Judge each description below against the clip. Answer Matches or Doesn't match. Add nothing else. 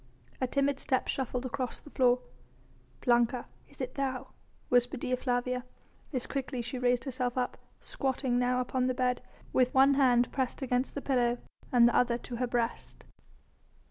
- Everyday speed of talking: Matches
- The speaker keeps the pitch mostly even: Matches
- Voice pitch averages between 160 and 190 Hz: Doesn't match